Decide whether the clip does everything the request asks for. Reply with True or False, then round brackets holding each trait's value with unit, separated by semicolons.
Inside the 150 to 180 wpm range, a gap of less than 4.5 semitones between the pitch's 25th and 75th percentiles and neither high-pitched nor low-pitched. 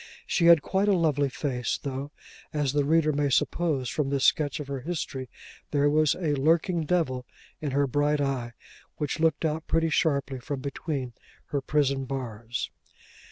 True (165 wpm; 2.7 semitones; 145 Hz)